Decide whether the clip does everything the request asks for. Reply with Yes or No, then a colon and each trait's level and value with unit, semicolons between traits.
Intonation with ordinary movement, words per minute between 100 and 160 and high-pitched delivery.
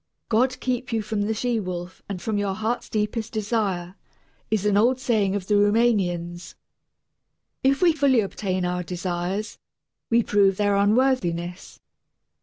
Yes: average, 3.9 semitones; average, 145 wpm; high, 205 Hz